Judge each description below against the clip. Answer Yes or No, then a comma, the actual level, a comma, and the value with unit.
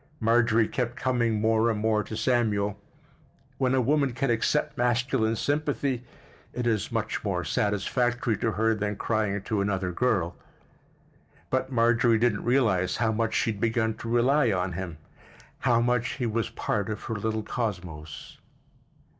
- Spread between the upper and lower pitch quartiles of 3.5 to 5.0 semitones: No, average, 2.7 semitones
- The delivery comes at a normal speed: Yes, average, 155 wpm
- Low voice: Yes, low, 115 Hz